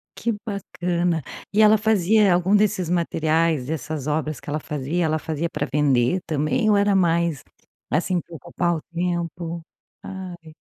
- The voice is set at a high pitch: No, medium, 170 Hz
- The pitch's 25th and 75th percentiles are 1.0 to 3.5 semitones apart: Yes, average, 3.2 semitones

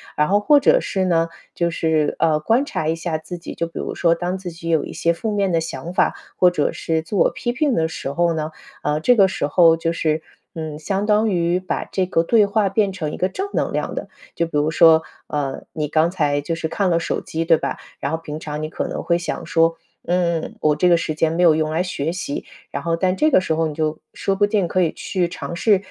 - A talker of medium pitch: Yes, medium, 170 Hz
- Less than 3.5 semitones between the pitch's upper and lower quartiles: Yes, average, 2.8 semitones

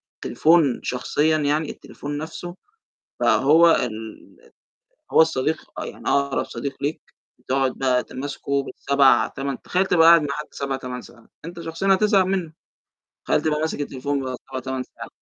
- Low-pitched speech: No, medium, 145 Hz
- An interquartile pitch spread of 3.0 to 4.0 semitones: Yes, average, 3.6 semitones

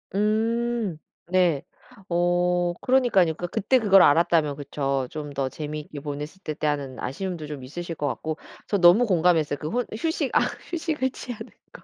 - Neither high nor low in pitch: Yes, medium, 175 Hz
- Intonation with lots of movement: Yes, wide, 6.0 semitones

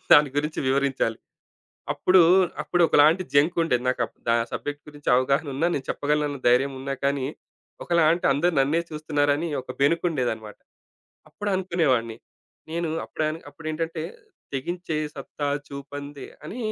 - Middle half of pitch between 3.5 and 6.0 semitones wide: No, average, 3.1 semitones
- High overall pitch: No, medium, 145 Hz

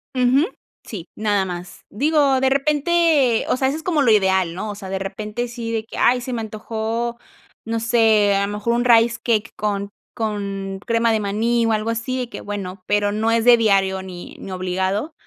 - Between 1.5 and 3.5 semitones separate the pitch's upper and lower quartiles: Yes, average, 3.1 semitones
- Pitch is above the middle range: Yes, high, 220 Hz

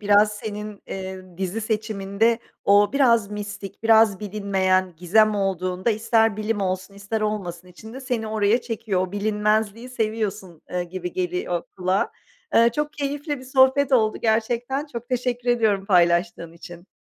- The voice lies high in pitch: Yes, high, 210 Hz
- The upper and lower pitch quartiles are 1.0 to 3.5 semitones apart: Yes, average, 3.2 semitones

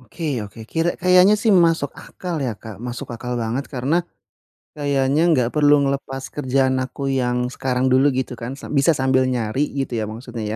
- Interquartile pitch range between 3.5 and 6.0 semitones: No, average, 2.8 semitones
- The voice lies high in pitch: No, low, 130 Hz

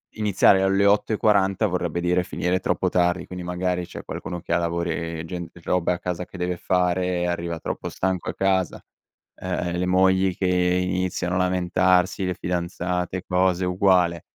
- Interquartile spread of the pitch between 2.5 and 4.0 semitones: No, narrow, 1.0 semitones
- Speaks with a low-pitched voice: Yes, very low, 90 Hz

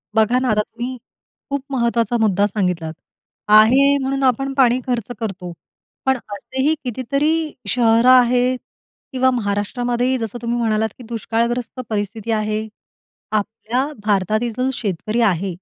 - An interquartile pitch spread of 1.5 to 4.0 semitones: Yes, average, 3.2 semitones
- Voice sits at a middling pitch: No, high, 235 Hz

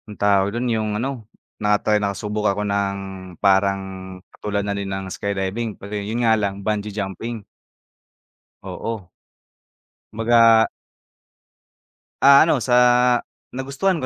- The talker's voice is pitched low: Yes, low, 105 Hz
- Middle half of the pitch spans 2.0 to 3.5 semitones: Yes, narrow, 2.4 semitones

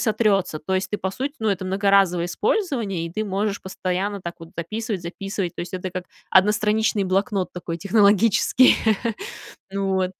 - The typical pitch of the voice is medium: No, high, 195 Hz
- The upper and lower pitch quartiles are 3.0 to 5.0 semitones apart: No, narrow, 2.6 semitones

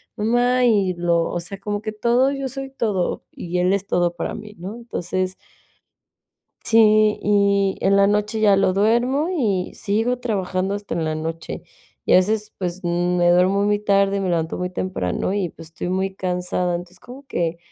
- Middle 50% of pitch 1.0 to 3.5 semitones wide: Yes, average, 3.2 semitones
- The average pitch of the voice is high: Yes, high, 195 Hz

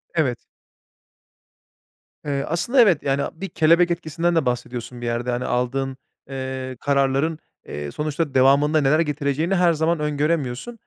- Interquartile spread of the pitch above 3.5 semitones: Yes, average, 3.9 semitones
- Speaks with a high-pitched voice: No, medium, 145 Hz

